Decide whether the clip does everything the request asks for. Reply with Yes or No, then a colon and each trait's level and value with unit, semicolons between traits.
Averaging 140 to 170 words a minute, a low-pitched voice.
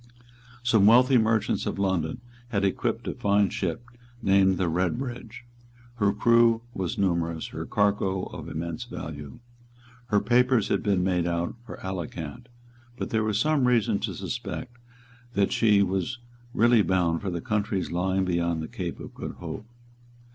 Yes: average, 155 wpm; low, 100 Hz